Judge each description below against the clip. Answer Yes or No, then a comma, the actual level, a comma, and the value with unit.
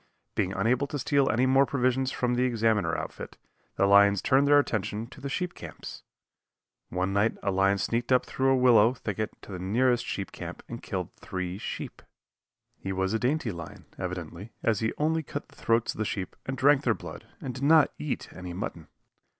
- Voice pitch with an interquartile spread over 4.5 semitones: Yes, average, 5.2 semitones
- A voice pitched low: Yes, low, 115 Hz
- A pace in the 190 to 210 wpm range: Yes, average, 200 wpm